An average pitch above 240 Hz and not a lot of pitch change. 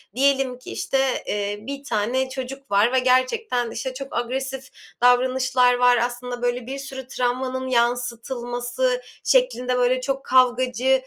Yes: very high, 255 Hz; narrow, 1.4 semitones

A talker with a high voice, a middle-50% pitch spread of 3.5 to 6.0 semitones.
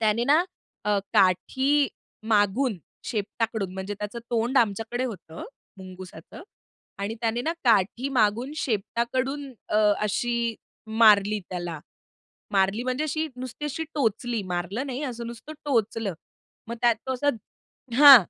Yes: high, 230 Hz; average, 4.0 semitones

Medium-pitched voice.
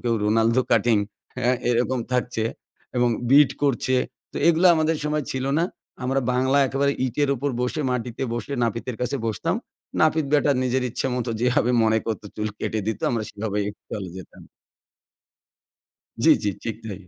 No: low, 125 Hz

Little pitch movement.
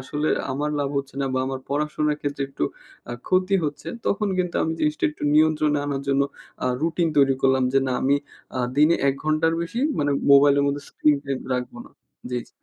Yes: narrow, 2.0 semitones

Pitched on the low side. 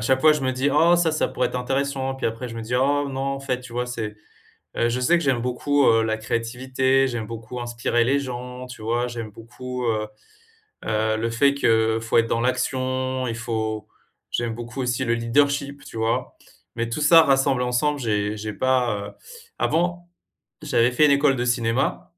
Yes: low, 125 Hz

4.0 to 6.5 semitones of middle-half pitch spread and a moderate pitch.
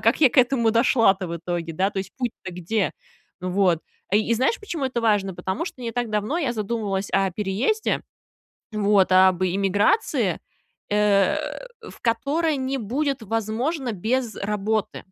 No: average, 4.5 semitones; high, 215 Hz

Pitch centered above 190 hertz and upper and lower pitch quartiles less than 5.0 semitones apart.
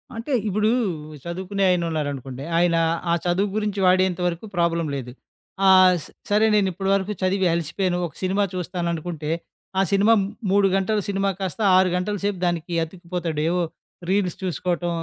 No: medium, 185 Hz; narrow, 2.5 semitones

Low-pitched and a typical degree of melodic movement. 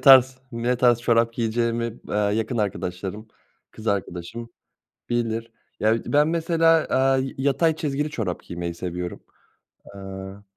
Yes: low, 115 Hz; average, 4.5 semitones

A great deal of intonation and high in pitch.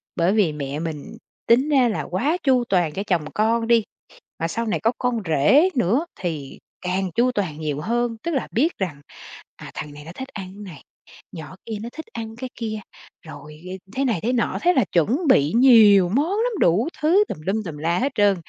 Yes: wide, 6.7 semitones; high, 210 Hz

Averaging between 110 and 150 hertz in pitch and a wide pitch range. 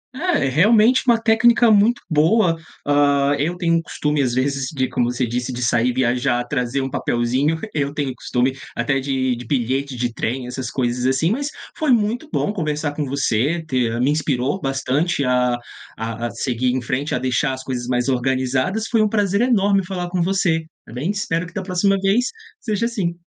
Yes: medium, 140 Hz; wide, 7.0 semitones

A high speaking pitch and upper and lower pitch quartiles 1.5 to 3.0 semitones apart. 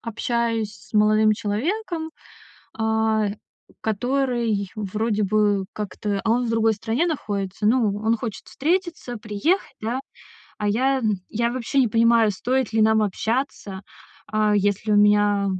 Yes: high, 220 Hz; narrow, 2.6 semitones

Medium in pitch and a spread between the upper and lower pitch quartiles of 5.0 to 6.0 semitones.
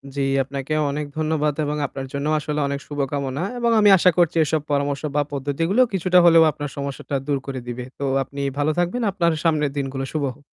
No: medium, 145 Hz; average, 2.7 semitones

